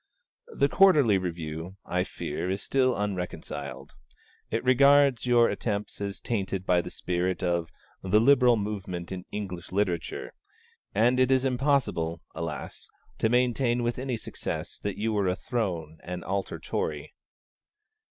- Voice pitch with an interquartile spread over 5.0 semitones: Yes, wide, 5.4 semitones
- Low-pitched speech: Yes, low, 100 Hz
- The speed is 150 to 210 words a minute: No, average, 140 wpm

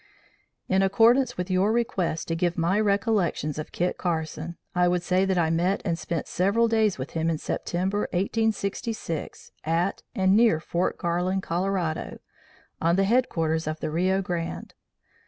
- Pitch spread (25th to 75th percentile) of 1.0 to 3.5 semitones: Yes, average, 3.0 semitones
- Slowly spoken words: No, average, 155 wpm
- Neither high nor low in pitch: Yes, medium, 180 Hz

